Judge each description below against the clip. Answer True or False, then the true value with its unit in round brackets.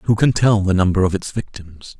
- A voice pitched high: False (100 Hz)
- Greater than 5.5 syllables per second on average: False (5.1 syllables/s)